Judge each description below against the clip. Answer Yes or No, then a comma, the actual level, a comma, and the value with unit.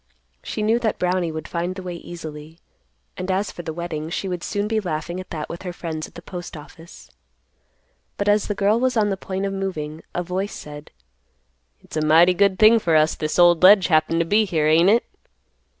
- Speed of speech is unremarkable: No, fast, 215 wpm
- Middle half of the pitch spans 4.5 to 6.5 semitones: No, average, 3.6 semitones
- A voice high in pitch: No, medium, 175 Hz